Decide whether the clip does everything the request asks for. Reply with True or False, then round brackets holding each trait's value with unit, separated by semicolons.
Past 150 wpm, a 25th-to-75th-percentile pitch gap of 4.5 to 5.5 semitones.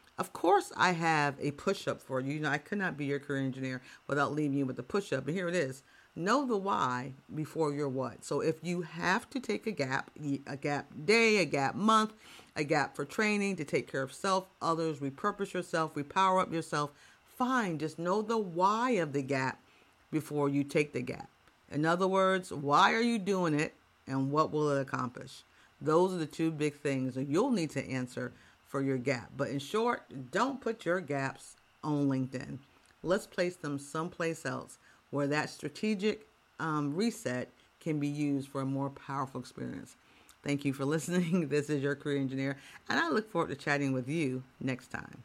True (200 wpm; 4.9 semitones)